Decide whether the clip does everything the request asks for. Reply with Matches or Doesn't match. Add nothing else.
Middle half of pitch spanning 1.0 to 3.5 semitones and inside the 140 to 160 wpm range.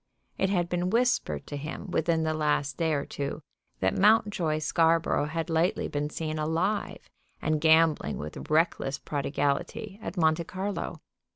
Matches